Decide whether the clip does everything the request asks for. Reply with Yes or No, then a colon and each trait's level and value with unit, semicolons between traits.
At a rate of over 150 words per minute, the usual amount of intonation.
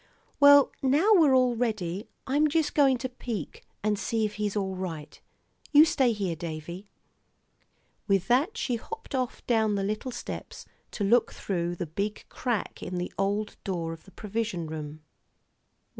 No: average, 160 wpm; wide, 5.8 semitones